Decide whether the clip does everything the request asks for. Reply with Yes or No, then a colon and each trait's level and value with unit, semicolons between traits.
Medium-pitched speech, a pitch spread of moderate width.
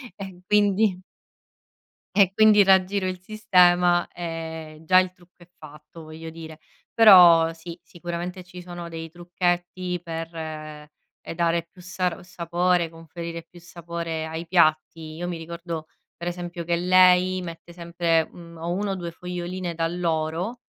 No: medium, 175 Hz; narrow, 1.7 semitones